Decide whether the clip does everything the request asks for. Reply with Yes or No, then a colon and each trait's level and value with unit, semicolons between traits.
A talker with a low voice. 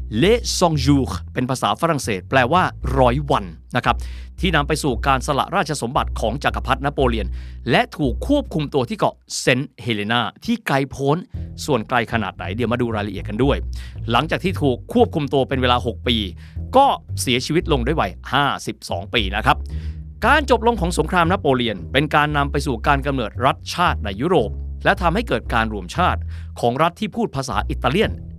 Yes: low, 125 Hz